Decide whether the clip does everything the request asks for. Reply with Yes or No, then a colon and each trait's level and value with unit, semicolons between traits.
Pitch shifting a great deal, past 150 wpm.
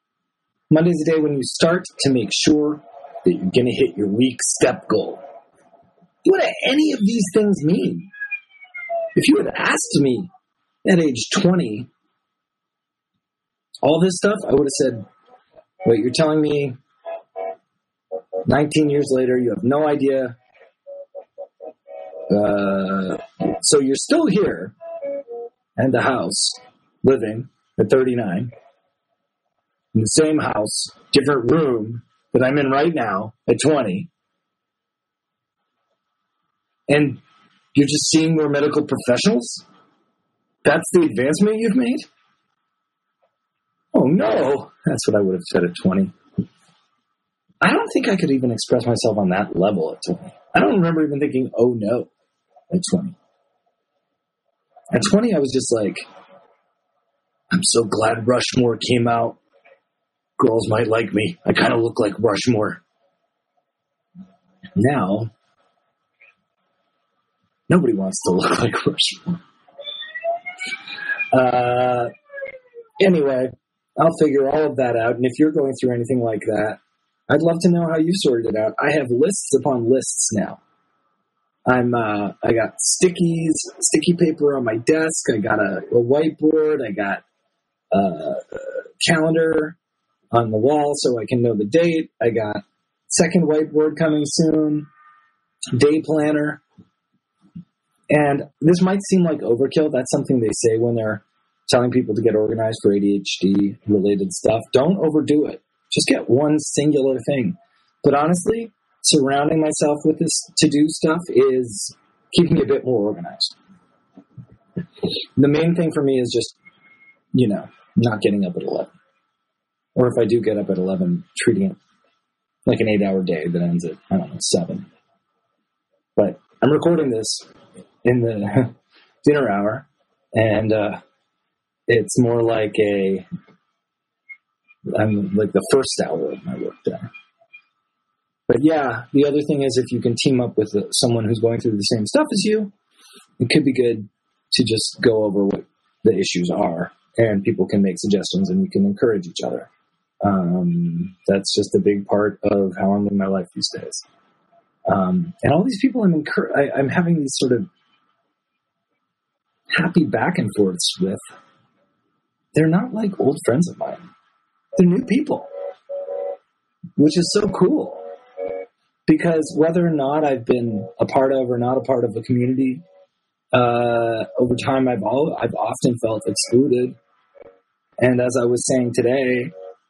No: wide, 7.1 semitones; average, 145 wpm